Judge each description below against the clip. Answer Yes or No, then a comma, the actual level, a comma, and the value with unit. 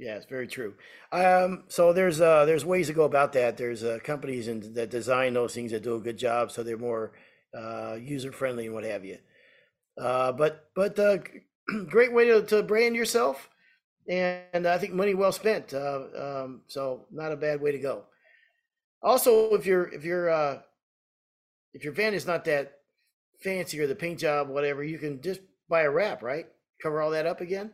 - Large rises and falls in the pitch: Yes, wide, 6.3 semitones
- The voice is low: No, medium, 155 Hz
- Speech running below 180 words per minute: No, average, 200 wpm